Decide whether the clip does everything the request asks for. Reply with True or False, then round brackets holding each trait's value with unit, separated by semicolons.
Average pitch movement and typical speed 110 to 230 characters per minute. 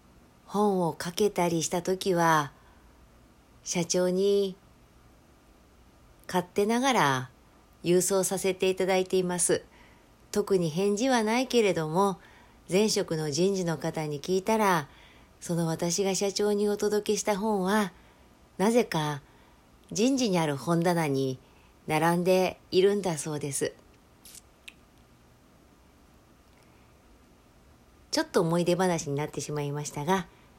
False (5.7 semitones; 215 characters per minute)